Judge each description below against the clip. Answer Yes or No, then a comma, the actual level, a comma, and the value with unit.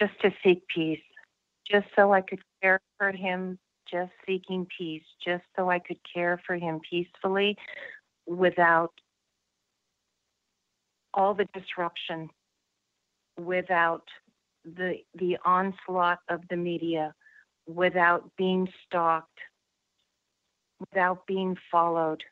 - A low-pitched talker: No, medium, 180 Hz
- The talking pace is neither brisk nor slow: No, slow, 105 wpm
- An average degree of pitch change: No, narrow, 1.8 semitones